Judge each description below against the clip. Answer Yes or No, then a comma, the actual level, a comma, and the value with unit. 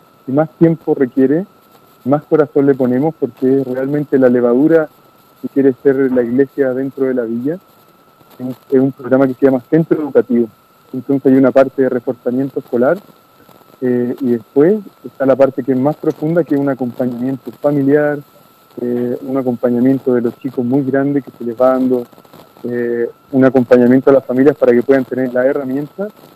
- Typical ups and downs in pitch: No, narrow, 2.2 semitones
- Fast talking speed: No, average, 175 wpm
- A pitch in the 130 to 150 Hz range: Yes, low, 135 Hz